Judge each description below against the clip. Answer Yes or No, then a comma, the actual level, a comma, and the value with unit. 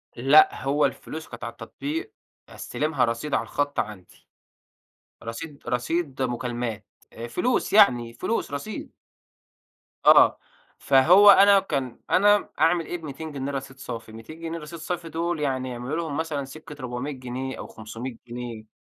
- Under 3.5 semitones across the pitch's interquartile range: No, average, 5.0 semitones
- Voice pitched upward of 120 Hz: Yes, medium, 140 Hz